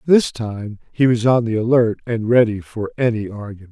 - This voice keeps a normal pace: Yes, average, 195 wpm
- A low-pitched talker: Yes, low, 115 Hz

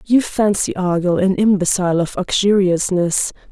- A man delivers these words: No, female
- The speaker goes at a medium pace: No, slow, 120 wpm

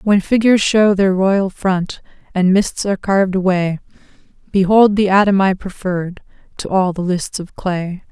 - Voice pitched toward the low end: No, high, 190 Hz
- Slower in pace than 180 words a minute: Yes, average, 165 wpm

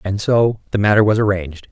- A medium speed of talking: No, fast, 210 wpm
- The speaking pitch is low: Yes, low, 100 Hz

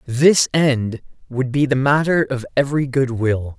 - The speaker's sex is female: No, male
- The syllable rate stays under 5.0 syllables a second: Yes, 4.3 syllables/s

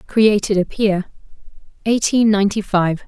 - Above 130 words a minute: No, slow, 115 wpm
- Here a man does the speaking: No, female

